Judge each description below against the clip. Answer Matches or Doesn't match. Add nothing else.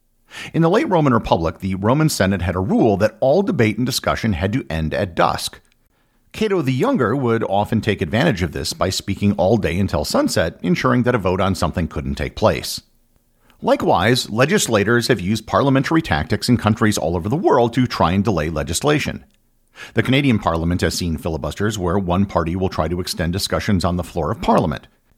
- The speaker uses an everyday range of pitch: Matches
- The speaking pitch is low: Matches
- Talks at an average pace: Matches